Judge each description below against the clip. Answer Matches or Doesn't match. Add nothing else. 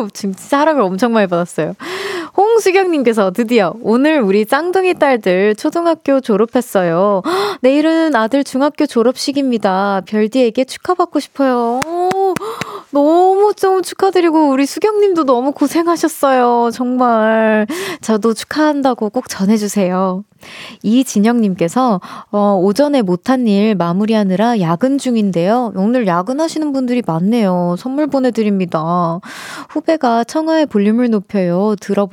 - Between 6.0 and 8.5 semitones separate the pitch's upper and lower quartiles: Matches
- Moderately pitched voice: Doesn't match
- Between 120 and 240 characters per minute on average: Doesn't match